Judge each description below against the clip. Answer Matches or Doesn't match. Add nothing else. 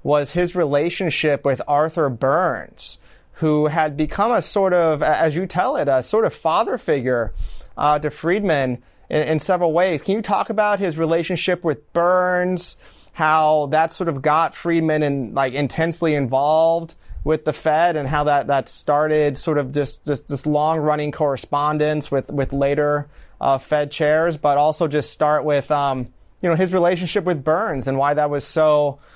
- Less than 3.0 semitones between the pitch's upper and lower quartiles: Matches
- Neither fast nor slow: Matches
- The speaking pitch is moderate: Matches